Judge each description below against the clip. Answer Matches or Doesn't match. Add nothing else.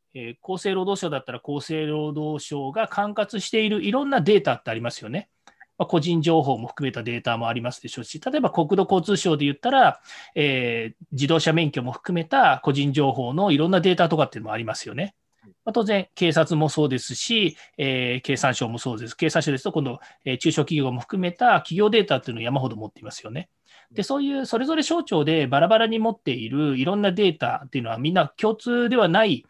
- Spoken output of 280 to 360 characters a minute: Doesn't match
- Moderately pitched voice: Matches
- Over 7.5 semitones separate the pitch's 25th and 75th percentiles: Doesn't match